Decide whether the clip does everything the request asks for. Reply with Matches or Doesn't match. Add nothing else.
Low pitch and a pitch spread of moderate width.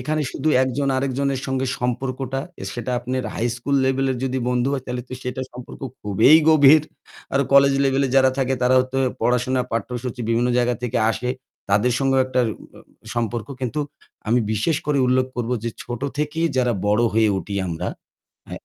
Doesn't match